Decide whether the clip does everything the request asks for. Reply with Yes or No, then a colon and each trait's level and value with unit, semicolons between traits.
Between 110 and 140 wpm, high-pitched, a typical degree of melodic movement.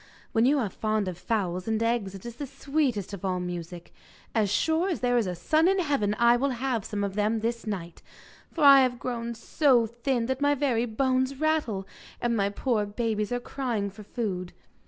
No: fast, 205 wpm; high, 230 Hz; average, 4.4 semitones